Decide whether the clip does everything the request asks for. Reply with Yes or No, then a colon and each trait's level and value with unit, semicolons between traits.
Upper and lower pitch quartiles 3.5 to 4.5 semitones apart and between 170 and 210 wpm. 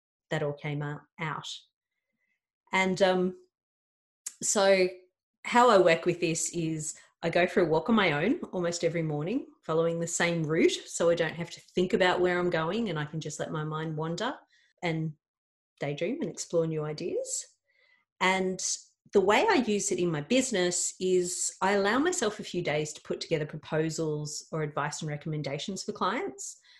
Yes: average, 4.0 semitones; average, 175 wpm